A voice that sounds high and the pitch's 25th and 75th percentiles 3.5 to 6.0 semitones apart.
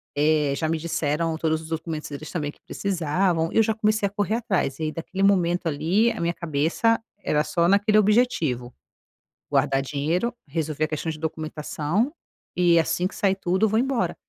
No: medium, 165 Hz; average, 4.5 semitones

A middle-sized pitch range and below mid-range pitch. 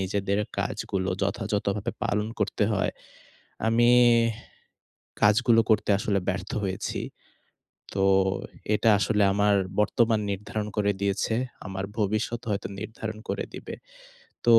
No: narrow, 1.8 semitones; low, 105 Hz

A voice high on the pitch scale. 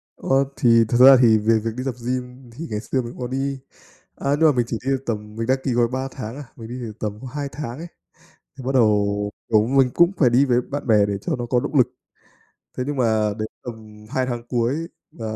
No: low, 125 Hz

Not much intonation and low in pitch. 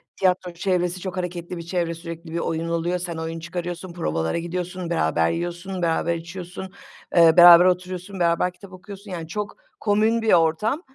No: narrow, 1.6 semitones; medium, 175 Hz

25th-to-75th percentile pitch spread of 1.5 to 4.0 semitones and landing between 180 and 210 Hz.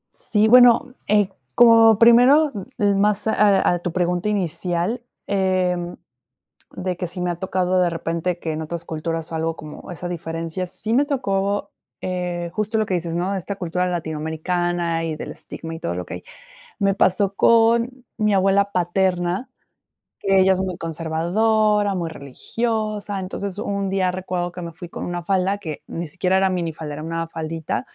Yes: average, 3.3 semitones; medium, 185 Hz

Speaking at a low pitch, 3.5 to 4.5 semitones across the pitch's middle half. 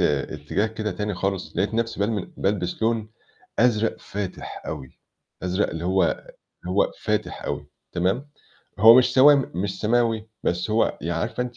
Yes: low, 105 Hz; average, 3.9 semitones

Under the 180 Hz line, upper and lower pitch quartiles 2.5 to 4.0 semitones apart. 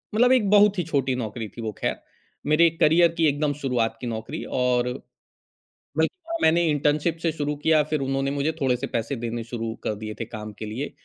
No: medium, 140 Hz; average, 5.3 semitones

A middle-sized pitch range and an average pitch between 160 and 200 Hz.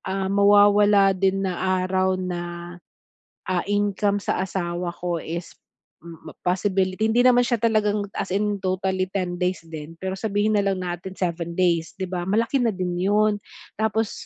No: narrow, 2.2 semitones; high, 190 Hz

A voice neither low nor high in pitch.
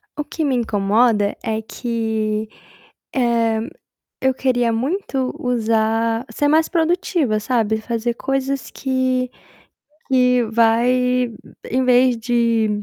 No: high, 245 Hz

